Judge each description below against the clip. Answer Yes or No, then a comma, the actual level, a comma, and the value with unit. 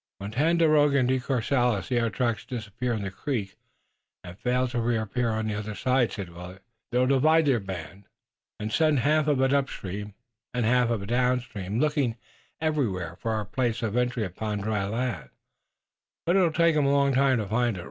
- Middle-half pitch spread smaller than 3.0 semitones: No, average, 4.4 semitones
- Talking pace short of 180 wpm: No, average, 185 wpm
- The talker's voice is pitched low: Yes, low, 120 Hz